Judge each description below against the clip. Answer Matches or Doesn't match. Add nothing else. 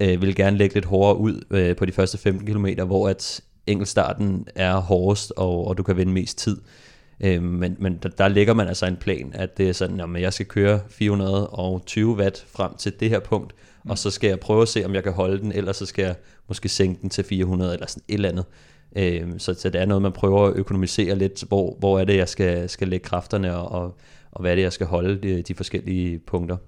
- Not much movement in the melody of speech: Matches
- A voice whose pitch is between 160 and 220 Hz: Doesn't match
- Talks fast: Matches